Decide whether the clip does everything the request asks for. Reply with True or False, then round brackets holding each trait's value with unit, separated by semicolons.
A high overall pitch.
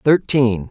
False (125 Hz)